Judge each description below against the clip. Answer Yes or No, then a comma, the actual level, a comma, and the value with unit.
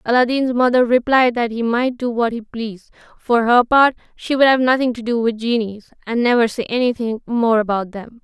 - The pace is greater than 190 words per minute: Yes, fast, 205 wpm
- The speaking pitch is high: Yes, high, 235 Hz